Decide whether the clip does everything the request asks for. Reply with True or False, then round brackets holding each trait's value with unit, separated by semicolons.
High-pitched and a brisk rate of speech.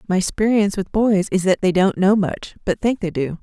True (195 Hz; 245 wpm)